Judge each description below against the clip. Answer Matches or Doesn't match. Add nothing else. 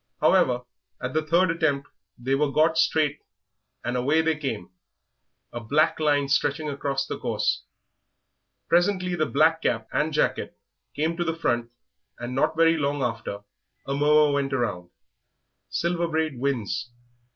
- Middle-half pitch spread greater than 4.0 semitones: Doesn't match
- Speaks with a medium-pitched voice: Matches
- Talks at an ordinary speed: Matches